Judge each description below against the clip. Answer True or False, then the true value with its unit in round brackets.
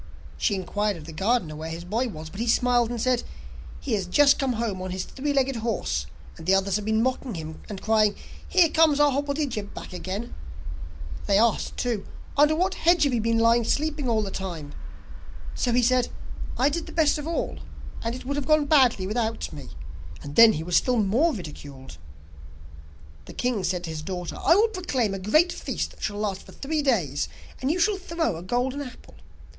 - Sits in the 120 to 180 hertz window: False (230 Hz)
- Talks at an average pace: False (210 wpm)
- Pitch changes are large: True (6.7 semitones)